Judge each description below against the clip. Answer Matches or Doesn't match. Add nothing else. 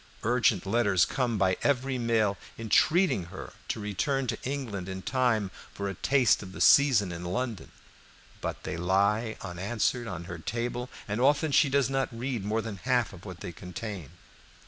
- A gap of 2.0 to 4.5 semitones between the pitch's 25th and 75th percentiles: Doesn't match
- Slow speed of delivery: Doesn't match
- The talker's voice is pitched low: Matches